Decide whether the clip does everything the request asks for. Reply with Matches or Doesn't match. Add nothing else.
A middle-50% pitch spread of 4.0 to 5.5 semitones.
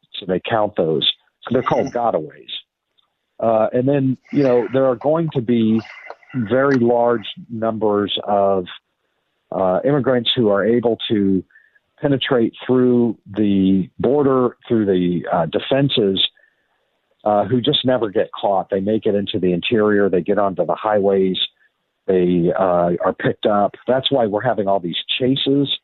Matches